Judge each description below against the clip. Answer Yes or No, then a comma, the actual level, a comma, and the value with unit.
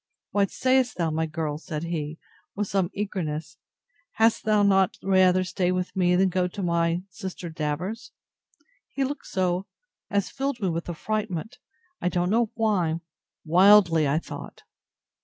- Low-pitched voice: No, medium, 185 Hz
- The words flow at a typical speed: Yes, average, 150 wpm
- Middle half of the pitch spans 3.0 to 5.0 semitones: Yes, average, 3.5 semitones